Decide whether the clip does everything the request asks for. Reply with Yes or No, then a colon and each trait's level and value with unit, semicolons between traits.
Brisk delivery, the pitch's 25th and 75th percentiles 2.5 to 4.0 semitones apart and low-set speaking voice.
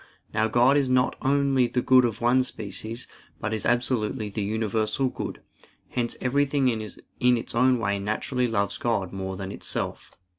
No: average, 160 wpm; average, 3.1 semitones; low, 120 Hz